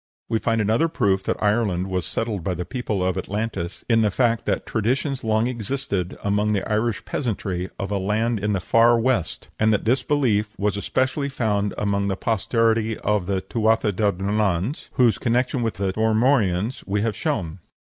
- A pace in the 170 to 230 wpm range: Yes, average, 180 wpm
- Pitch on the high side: No, low, 105 Hz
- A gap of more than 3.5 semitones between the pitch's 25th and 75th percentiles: No, average, 2.8 semitones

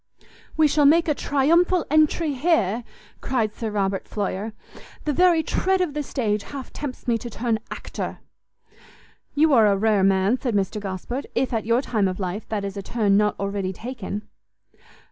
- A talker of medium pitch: No, high, 230 Hz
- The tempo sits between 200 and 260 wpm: No, average, 175 wpm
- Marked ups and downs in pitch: Yes, wide, 6.2 semitones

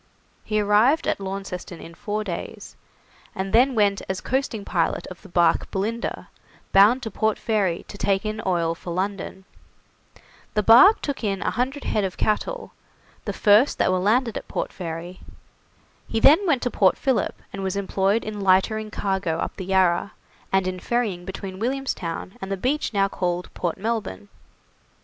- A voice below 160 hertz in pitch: No, high, 200 Hz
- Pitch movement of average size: Yes, average, 3.2 semitones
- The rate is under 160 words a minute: No, average, 170 wpm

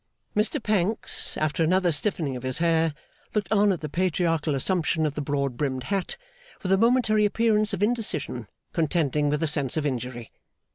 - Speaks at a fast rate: No, average, 175 wpm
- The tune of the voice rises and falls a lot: Yes, wide, 5.8 semitones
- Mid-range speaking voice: Yes, medium, 165 Hz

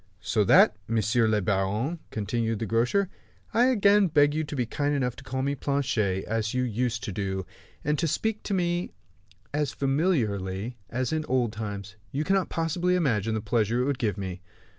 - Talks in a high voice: No, low, 125 Hz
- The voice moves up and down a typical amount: No, wide, 5.9 semitones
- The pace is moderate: Yes, average, 185 wpm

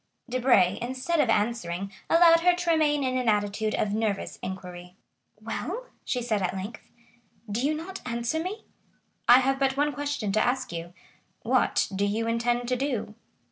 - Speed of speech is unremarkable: Yes, average, 165 wpm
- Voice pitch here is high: Yes, high, 240 Hz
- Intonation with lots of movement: Yes, wide, 5.9 semitones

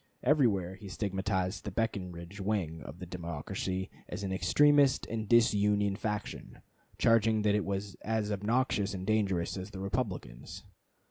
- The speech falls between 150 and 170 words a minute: No, average, 140 wpm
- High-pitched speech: No, low, 100 Hz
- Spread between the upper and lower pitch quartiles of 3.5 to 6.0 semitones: No, narrow, 2.6 semitones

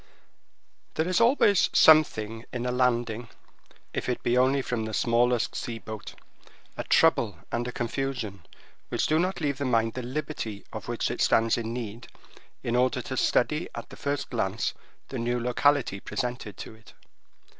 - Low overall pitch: Yes, low, 125 Hz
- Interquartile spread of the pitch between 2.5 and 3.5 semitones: Yes, average, 3.1 semitones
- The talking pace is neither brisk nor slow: Yes, average, 165 wpm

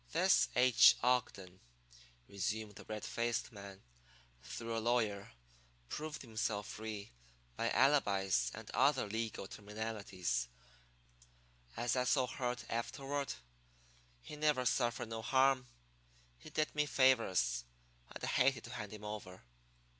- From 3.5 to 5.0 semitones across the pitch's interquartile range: Yes, average, 4.0 semitones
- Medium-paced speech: No, slow, 125 wpm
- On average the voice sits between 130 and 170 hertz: No, low, 115 Hz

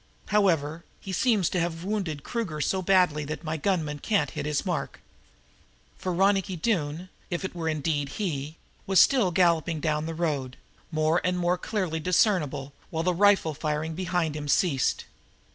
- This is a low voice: No, medium, 170 Hz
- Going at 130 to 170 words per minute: Yes, average, 160 wpm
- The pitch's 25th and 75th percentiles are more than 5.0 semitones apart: No, average, 3.6 semitones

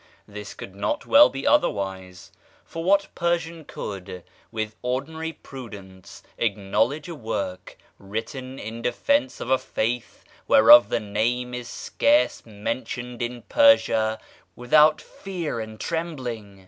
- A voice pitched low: Yes, low, 120 Hz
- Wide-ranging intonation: Yes, wide, 6.6 semitones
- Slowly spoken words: Yes, slow, 120 wpm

